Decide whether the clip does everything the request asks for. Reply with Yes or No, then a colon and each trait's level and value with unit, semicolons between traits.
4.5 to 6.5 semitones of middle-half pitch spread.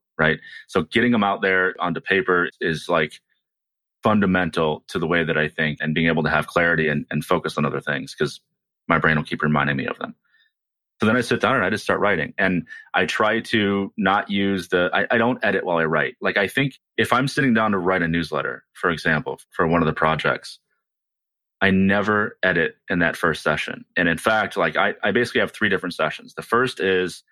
Yes: average, 5.1 semitones